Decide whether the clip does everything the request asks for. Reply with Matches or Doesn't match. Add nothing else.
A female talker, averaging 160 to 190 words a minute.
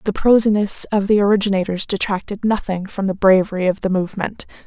Matches